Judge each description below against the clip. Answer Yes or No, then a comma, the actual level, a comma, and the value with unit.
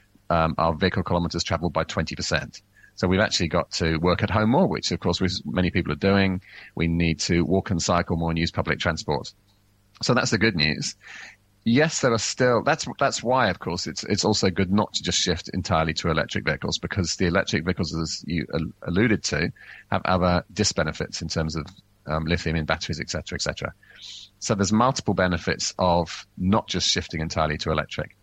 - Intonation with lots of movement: No, average, 3.3 semitones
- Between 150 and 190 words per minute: No, average, 200 wpm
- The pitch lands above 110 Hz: No, very low, 90 Hz